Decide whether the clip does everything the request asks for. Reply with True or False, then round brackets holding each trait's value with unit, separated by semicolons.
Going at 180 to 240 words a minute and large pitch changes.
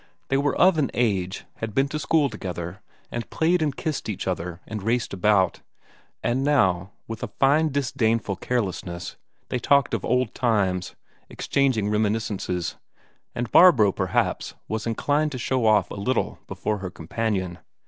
False (155 wpm; 5.7 semitones)